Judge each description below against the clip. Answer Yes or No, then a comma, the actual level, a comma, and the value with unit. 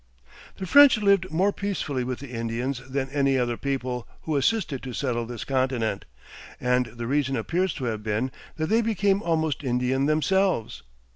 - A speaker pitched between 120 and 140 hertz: Yes, low, 135 Hz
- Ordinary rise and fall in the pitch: No, wide, 5.7 semitones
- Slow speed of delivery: No, average, 165 wpm